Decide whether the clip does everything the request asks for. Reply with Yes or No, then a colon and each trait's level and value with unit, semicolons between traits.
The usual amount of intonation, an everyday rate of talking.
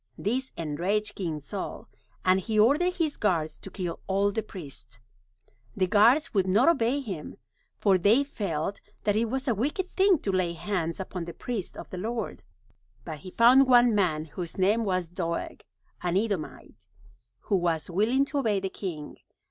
Yes: average, 4.9 semitones; average, 170 wpm